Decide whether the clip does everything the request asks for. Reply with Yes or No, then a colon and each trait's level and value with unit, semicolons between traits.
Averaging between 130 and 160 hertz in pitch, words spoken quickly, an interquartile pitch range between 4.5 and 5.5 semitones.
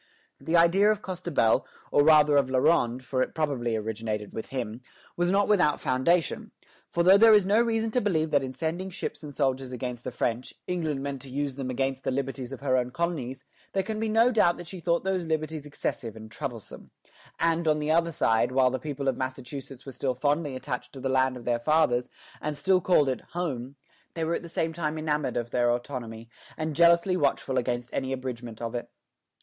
Yes: medium, 140 Hz; fast, 210 wpm; average, 4.9 semitones